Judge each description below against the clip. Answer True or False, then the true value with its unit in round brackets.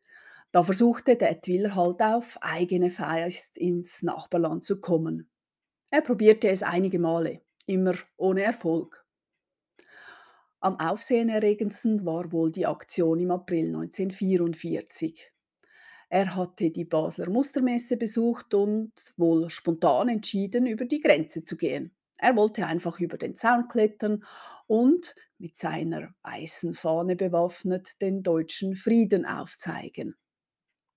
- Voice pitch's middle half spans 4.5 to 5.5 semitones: True (5.0 semitones)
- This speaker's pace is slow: True (120 wpm)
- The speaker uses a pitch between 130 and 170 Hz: False (190 Hz)